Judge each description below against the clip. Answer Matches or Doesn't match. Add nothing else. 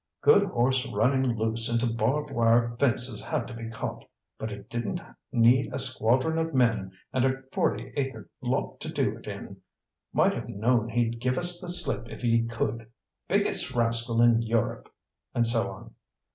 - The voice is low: Matches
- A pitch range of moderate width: Doesn't match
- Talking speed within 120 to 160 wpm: Doesn't match